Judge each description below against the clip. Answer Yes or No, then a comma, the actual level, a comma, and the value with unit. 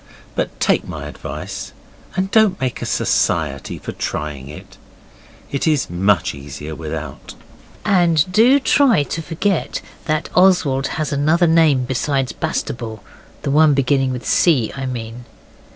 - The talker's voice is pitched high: No, medium, 140 Hz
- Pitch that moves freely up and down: Yes, wide, 6.8 semitones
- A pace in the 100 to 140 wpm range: Yes, slow, 135 wpm